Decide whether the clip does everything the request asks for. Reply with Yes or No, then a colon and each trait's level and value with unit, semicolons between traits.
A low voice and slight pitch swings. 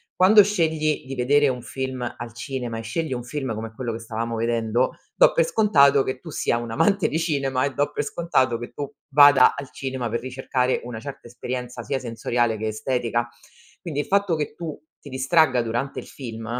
No: low, 130 Hz; average, 3.5 semitones